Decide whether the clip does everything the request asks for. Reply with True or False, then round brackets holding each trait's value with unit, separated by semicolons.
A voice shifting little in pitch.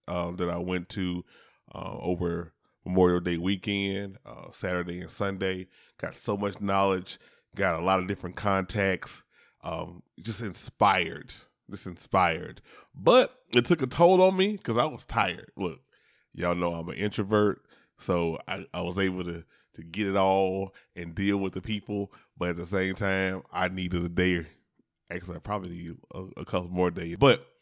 True (2.2 semitones)